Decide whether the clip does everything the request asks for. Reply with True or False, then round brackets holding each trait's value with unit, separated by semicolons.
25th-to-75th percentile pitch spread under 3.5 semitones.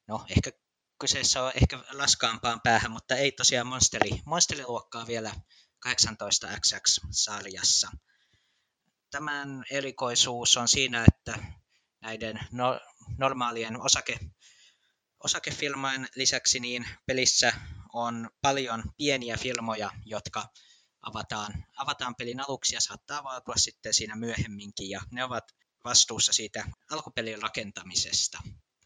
True (2.8 semitones)